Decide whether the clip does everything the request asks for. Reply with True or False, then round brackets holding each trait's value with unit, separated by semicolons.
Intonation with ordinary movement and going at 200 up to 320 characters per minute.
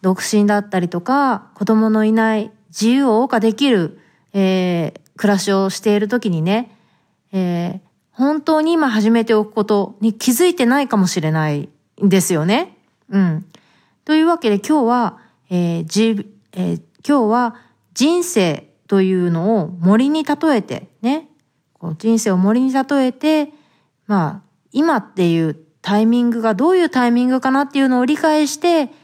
False (5.8 semitones; 295 characters per minute)